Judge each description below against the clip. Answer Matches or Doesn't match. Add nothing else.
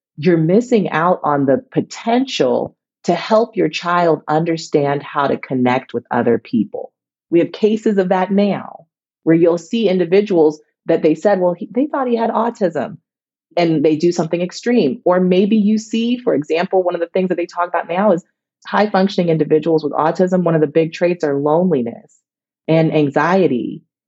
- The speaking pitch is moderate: Matches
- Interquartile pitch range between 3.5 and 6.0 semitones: Matches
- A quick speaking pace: Doesn't match